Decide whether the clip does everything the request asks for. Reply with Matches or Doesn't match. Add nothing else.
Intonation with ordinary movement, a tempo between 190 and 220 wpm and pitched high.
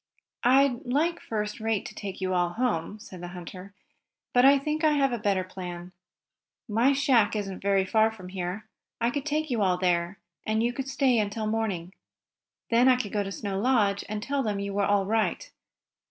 Matches